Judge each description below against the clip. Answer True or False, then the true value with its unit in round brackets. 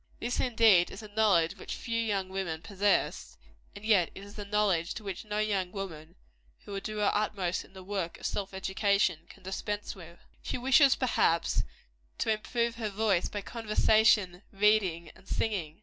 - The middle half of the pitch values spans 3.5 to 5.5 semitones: False (2.7 semitones)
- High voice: True (200 Hz)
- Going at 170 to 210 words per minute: True (175 wpm)